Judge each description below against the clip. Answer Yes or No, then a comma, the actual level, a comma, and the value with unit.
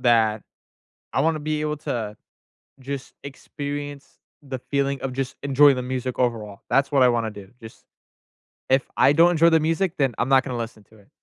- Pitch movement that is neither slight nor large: Yes, average, 3.3 semitones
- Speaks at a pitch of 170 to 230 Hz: No, low, 135 Hz